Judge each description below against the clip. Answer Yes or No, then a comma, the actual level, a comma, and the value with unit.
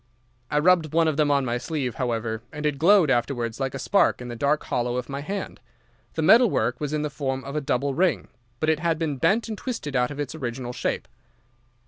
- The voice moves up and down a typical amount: Yes, average, 4.1 semitones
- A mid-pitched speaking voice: Yes, medium, 145 Hz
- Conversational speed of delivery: No, fast, 230 wpm